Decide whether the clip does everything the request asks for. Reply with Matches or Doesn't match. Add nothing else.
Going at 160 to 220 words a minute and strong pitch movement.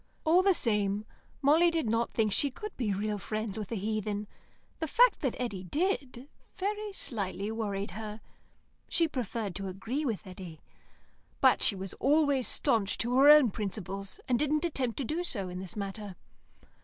Matches